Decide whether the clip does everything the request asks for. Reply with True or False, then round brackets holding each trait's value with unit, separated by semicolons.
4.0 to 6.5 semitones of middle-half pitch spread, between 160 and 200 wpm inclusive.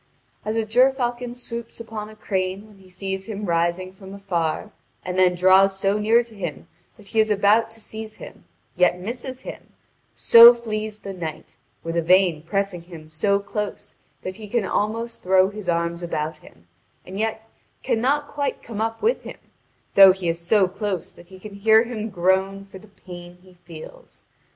False (3.3 semitones; 180 wpm)